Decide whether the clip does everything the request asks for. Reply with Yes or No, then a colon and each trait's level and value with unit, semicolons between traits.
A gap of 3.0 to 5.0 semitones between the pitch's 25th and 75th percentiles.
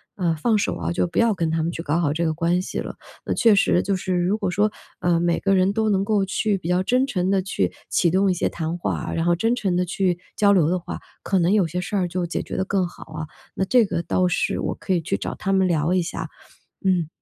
No: narrow, 2.5 semitones